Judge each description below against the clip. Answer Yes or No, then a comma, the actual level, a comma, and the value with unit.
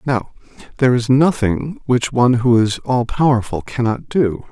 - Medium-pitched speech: No, low, 125 Hz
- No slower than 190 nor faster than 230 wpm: No, average, 160 wpm